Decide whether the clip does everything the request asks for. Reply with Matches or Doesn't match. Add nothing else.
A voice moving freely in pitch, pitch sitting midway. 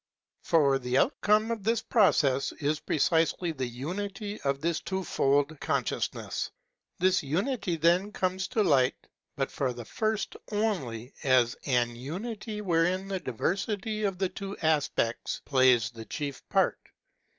Matches